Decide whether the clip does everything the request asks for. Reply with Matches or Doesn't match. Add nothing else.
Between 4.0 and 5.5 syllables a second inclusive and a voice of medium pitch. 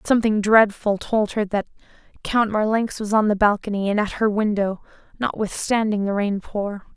Doesn't match